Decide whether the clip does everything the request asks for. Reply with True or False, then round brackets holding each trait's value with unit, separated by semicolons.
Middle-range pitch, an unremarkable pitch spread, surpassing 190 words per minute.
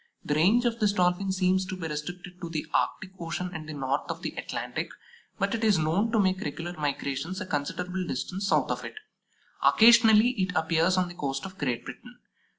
True (180 Hz; 3.8 semitones; 200 wpm)